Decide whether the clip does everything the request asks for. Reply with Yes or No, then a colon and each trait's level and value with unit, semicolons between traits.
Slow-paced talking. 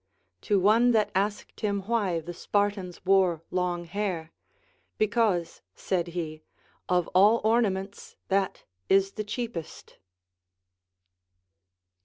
Yes: slow, 105 wpm